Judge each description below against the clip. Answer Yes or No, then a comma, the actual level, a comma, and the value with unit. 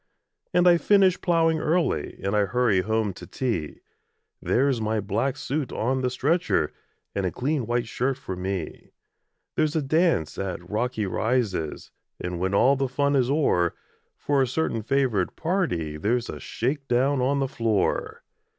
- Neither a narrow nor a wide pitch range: No, wide, 5.8 semitones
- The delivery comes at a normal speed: Yes, average, 160 wpm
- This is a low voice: Yes, low, 125 Hz